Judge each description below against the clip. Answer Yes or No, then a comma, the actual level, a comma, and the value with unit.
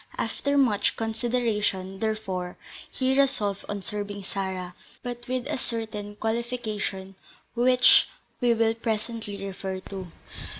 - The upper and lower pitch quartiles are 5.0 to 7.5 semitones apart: No, average, 3.5 semitones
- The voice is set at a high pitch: Yes, high, 220 Hz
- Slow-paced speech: Yes, slow, 115 wpm